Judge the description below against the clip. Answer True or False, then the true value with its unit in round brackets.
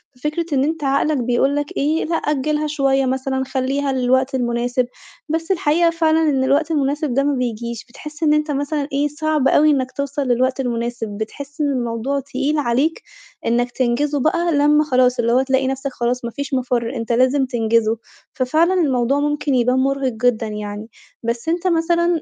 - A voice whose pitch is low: False (270 Hz)